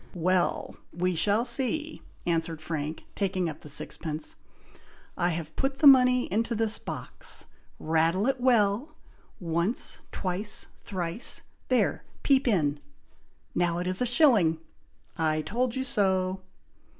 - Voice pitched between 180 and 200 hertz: Yes, high, 190 Hz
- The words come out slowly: Yes, slow, 125 wpm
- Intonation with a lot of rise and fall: Yes, wide, 6.7 semitones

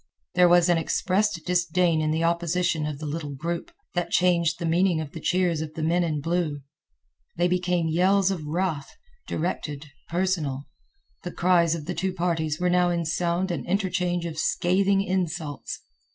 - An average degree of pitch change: No, narrow, 2.2 semitones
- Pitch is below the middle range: No, medium, 170 Hz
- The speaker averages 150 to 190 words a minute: Yes, average, 170 wpm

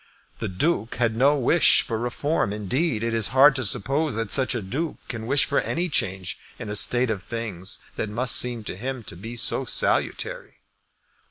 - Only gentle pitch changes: No, average, 4.0 semitones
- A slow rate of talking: No, average, 190 wpm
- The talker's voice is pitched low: Yes, low, 115 Hz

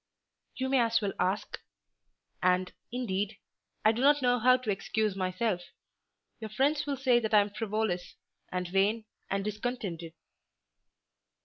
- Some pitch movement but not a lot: Yes, average, 4.2 semitones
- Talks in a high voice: Yes, high, 215 Hz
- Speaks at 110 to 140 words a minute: Yes, slow, 135 wpm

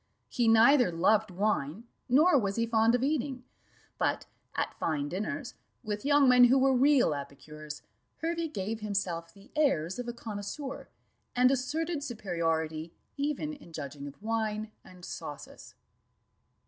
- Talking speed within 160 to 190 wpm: No, average, 140 wpm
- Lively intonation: Yes, wide, 7.4 semitones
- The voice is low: No, high, 225 Hz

